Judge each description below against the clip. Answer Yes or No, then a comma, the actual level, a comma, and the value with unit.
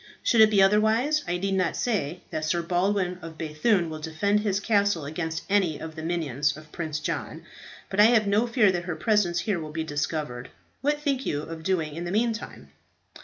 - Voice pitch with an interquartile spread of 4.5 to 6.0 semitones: Yes, average, 4.9 semitones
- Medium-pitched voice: Yes, medium, 175 Hz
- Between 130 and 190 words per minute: No, fast, 205 wpm